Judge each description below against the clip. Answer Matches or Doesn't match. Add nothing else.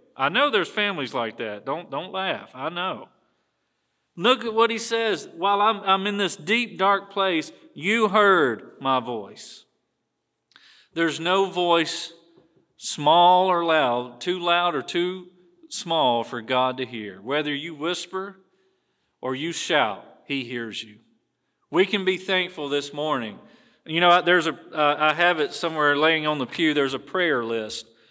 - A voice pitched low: Doesn't match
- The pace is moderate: Matches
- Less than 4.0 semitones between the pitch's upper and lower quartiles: Doesn't match